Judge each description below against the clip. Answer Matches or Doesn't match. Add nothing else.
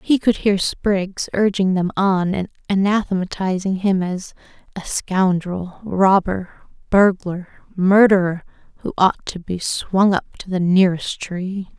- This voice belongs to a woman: Matches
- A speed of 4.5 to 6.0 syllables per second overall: Doesn't match